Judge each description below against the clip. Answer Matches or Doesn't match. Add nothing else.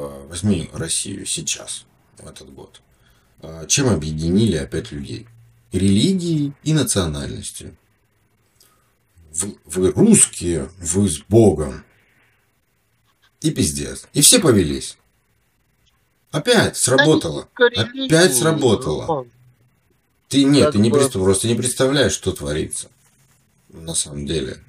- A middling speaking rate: Doesn't match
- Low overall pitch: Matches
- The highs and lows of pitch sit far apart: Matches